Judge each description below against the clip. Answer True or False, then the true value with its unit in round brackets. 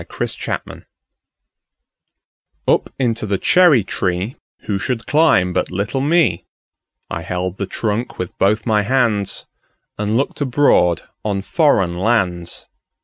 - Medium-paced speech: False (110 wpm)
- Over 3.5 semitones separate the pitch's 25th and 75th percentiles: True (5.6 semitones)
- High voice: False (105 Hz)